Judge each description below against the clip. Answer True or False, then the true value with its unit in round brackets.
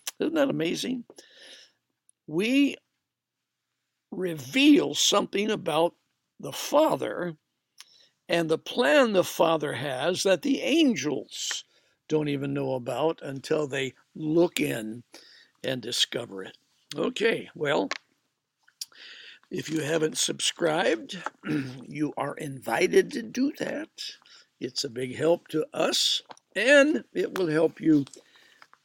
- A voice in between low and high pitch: True (165 Hz)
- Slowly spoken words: True (110 wpm)